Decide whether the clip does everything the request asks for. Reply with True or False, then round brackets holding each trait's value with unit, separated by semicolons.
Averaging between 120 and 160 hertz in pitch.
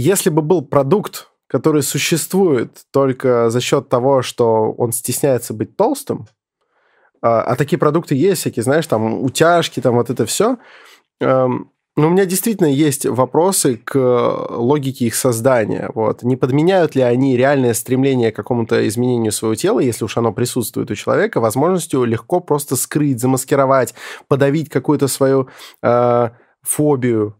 True (130 Hz)